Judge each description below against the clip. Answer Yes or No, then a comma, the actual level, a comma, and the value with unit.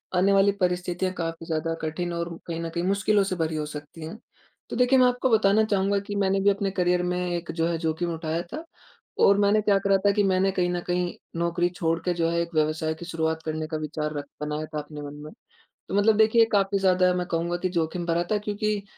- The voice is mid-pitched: Yes, medium, 180 Hz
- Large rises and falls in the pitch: No, average, 3.3 semitones